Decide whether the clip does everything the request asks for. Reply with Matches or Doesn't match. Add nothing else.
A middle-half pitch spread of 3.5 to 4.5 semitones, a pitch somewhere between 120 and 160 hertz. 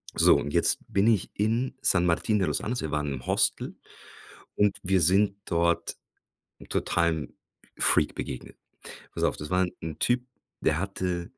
Doesn't match